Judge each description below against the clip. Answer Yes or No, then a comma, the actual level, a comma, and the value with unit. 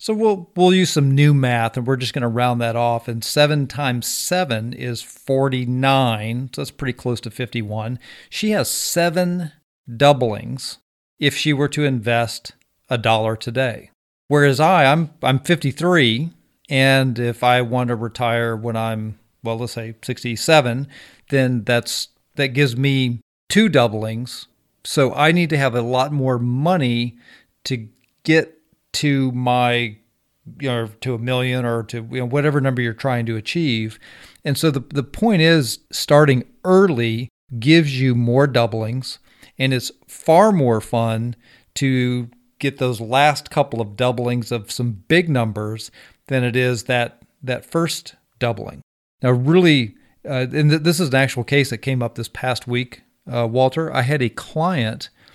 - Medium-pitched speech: No, low, 125 Hz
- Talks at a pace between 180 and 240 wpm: No, average, 160 wpm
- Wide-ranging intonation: No, average, 3.5 semitones